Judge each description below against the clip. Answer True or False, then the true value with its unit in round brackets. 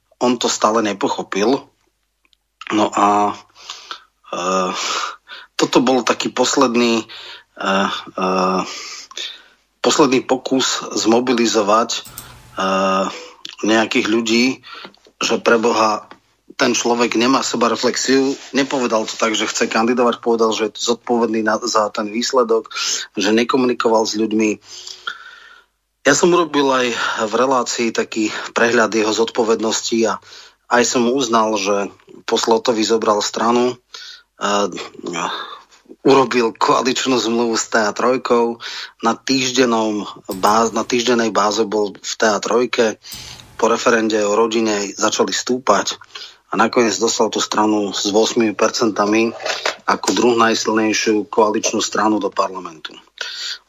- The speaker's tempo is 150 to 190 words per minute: False (110 wpm)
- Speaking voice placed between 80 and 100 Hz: False (115 Hz)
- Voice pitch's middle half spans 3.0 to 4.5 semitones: False (2.5 semitones)